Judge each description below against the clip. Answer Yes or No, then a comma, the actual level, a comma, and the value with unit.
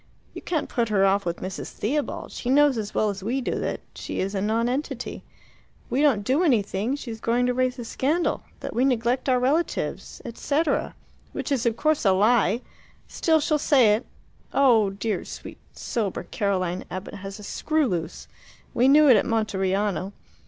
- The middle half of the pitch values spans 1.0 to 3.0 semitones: No, average, 5.1 semitones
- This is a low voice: No, high, 230 Hz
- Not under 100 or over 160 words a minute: No, average, 180 wpm